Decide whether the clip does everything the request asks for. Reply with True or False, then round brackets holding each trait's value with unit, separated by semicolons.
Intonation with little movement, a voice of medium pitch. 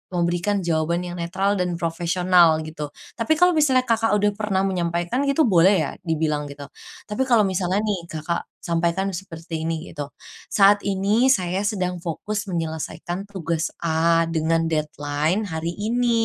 False (3.3 semitones; 175 Hz)